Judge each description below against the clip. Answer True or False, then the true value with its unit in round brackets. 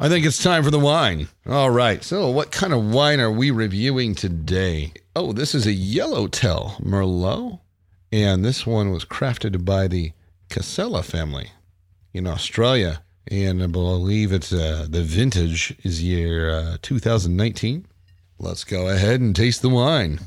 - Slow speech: False (155 wpm)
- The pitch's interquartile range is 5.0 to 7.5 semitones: True (5.3 semitones)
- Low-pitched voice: True (95 Hz)